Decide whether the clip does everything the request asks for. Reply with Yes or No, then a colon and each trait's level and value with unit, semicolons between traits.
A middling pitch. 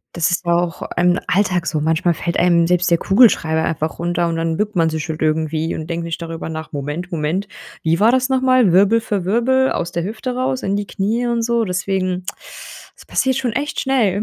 Yes: medium, 180 Hz